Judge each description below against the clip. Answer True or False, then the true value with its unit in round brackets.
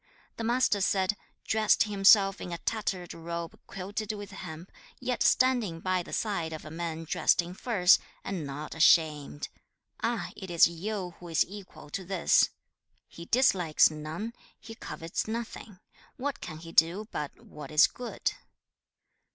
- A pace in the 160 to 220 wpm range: False (150 wpm)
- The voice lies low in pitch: False (185 Hz)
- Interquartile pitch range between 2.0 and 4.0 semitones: False (4.4 semitones)